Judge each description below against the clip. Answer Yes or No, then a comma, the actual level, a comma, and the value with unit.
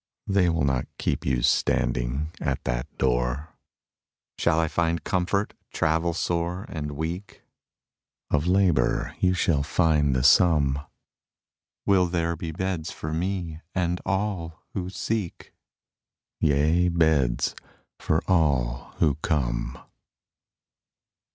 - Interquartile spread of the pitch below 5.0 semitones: Yes, average, 3.8 semitones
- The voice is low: Yes, very low, 80 Hz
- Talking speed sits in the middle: No, slow, 110 wpm